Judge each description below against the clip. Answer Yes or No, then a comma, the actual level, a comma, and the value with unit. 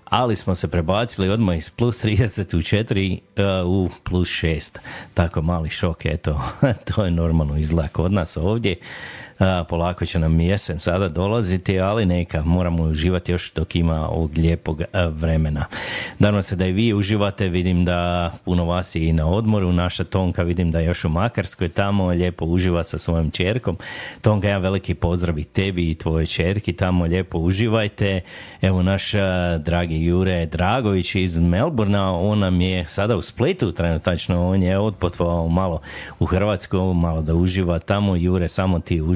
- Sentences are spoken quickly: Yes, fast, 165 wpm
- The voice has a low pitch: Yes, very low, 90 Hz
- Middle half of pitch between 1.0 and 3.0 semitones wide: Yes, narrow, 2.5 semitones